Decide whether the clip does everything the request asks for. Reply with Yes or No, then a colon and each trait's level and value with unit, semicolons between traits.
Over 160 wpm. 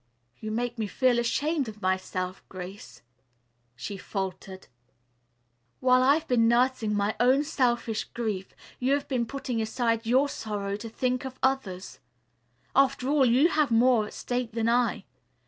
No: average, 145 wpm